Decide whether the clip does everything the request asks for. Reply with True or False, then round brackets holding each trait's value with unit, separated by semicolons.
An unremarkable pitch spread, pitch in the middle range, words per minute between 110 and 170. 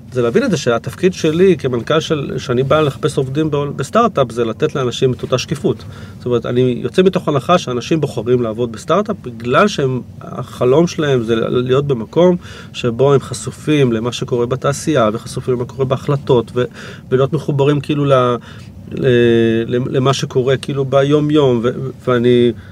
False (3.6 semitones; 130 Hz; 145 wpm)